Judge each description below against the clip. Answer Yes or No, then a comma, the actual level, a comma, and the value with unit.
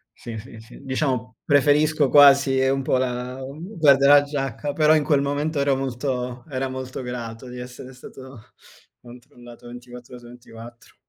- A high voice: No, low, 130 Hz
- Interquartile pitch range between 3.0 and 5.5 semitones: No, narrow, 2.5 semitones